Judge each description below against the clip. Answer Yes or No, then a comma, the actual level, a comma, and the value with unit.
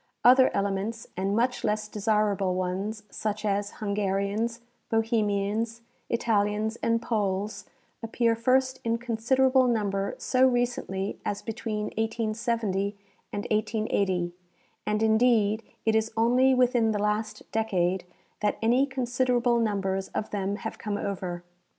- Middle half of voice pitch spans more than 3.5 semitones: No, narrow, 2.5 semitones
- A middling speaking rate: No, slow, 120 wpm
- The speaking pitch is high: Yes, high, 215 Hz